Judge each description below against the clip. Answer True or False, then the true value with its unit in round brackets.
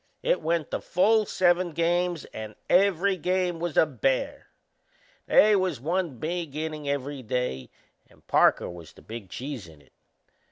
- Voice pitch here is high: False (160 Hz)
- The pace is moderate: True (155 wpm)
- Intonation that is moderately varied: False (5.8 semitones)